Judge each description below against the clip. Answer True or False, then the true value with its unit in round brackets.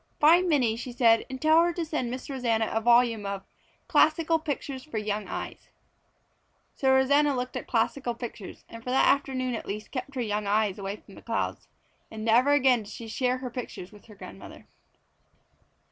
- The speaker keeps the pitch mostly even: False (3.7 semitones)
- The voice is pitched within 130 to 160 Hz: False (245 Hz)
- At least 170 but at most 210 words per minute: True (190 wpm)